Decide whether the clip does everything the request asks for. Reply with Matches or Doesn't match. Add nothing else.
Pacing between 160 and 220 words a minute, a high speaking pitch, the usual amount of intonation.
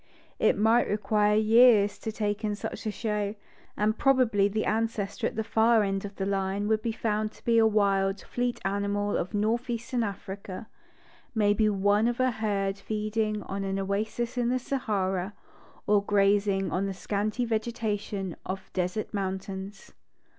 Doesn't match